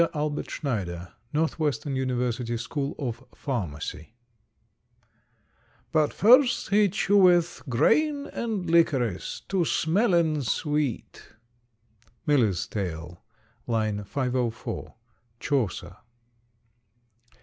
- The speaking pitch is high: No, medium, 140 Hz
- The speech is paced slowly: Yes, slow, 75 wpm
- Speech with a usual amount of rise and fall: No, wide, 6.7 semitones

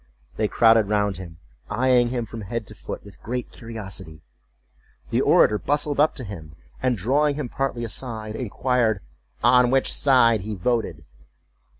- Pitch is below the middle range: Yes, low, 115 Hz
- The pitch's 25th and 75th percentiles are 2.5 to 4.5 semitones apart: Yes, average, 3.3 semitones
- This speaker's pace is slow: No, average, 155 wpm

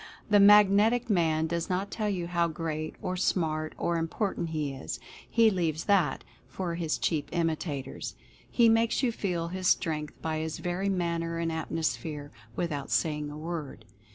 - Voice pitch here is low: No, medium, 170 Hz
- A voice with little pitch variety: No, average, 3.2 semitones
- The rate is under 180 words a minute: Yes, average, 165 wpm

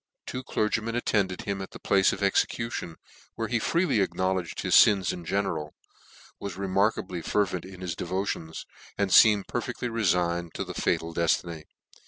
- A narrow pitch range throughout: No, average, 3.5 semitones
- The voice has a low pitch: Yes, very low, 95 Hz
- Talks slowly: No, average, 160 wpm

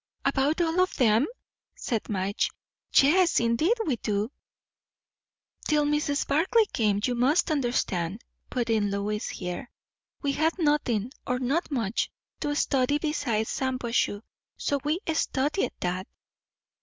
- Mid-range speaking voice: No, very high, 260 Hz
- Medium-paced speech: No, slow, 125 wpm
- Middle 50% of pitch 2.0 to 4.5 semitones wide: No, wide, 5.6 semitones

